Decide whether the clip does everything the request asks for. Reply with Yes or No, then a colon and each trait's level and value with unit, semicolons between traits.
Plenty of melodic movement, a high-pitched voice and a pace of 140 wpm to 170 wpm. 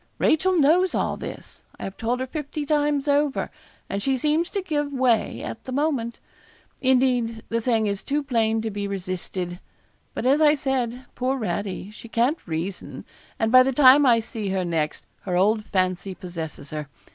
No: wide, 6.1 semitones; high, 235 Hz; average, 180 wpm